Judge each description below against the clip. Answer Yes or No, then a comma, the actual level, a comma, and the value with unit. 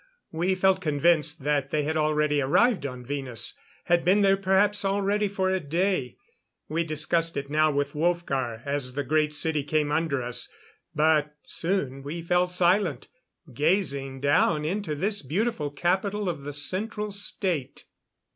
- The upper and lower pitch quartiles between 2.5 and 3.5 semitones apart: No, average, 4.7 semitones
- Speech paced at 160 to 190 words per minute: No, average, 150 wpm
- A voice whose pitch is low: No, medium, 155 Hz